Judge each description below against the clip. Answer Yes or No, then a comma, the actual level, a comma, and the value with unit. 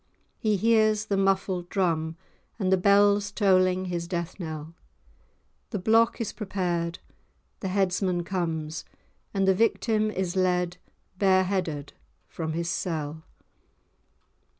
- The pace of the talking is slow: Yes, slow, 120 wpm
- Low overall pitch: No, medium, 185 Hz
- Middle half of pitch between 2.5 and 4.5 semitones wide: Yes, average, 2.8 semitones